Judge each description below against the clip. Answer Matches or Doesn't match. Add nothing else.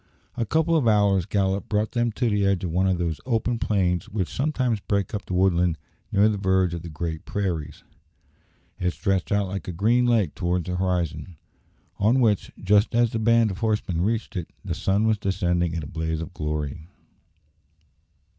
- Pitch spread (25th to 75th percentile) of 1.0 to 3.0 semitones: Doesn't match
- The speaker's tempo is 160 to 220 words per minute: Matches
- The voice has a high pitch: Doesn't match